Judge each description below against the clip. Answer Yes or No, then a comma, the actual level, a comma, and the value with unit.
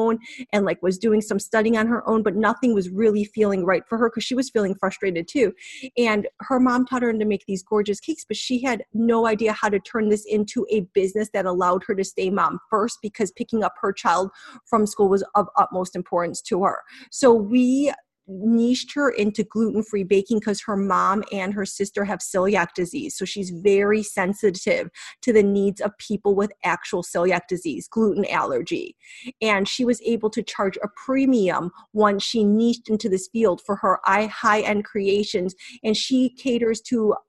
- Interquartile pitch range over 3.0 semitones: No, narrow, 2.6 semitones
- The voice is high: Yes, high, 210 Hz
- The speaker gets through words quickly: No, average, 195 wpm